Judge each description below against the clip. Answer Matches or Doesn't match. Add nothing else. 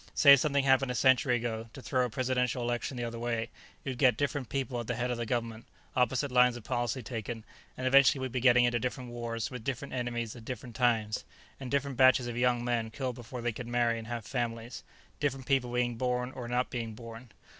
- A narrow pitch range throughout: Matches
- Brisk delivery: Matches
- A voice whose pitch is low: Matches